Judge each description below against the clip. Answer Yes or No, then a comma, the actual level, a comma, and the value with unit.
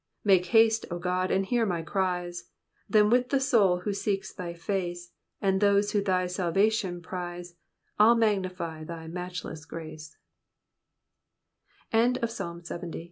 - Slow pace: Yes, slow, 120 wpm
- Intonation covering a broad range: No, average, 2.8 semitones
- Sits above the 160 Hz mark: Yes, medium, 185 Hz